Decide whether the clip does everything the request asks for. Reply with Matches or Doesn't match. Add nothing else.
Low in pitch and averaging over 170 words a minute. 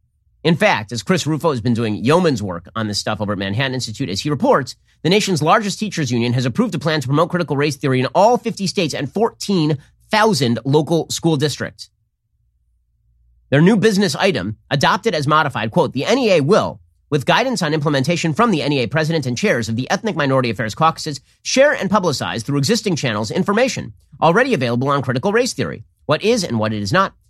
Doesn't match